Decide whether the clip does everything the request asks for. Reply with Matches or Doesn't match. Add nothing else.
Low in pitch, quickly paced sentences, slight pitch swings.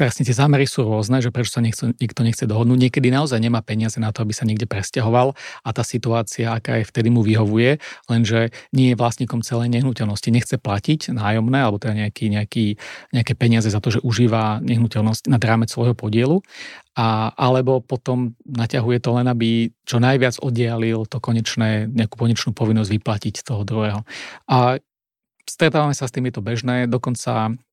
Matches